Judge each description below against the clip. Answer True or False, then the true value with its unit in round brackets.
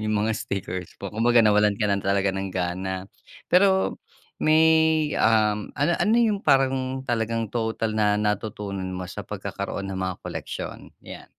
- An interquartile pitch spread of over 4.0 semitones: True (5.2 semitones)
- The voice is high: False (105 Hz)